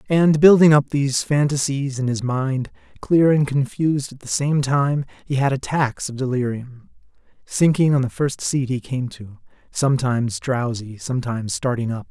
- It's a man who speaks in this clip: Yes, male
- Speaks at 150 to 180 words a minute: Yes, average, 160 wpm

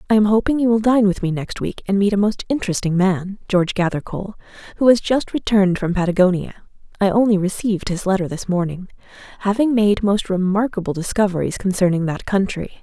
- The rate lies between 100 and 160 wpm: No, average, 180 wpm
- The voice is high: Yes, high, 195 Hz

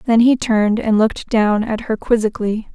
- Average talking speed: Yes, average, 195 wpm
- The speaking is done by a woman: Yes, female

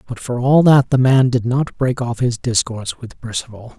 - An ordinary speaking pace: No, fast, 220 wpm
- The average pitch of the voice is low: Yes, low, 125 Hz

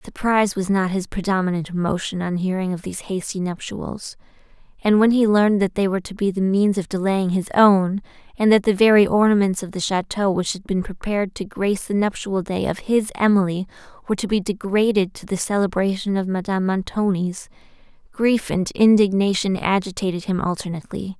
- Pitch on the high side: Yes, high, 195 Hz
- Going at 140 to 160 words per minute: No, average, 180 wpm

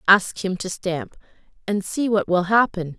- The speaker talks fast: No, average, 180 wpm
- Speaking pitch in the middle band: No, high, 195 Hz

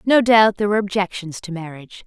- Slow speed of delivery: No, fast, 205 wpm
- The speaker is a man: No, female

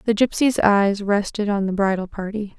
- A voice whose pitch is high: Yes, high, 205 Hz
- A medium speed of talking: Yes, average, 185 wpm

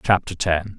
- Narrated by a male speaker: Yes, male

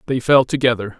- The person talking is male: Yes, male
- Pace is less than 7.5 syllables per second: Yes, 6.2 syllables/s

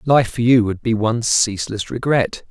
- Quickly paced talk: No, average, 190 wpm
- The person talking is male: Yes, male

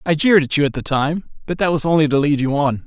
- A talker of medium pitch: Yes, medium, 150 Hz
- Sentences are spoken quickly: Yes, fast, 315 wpm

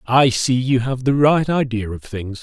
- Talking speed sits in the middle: No, fast, 225 wpm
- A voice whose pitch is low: Yes, low, 125 Hz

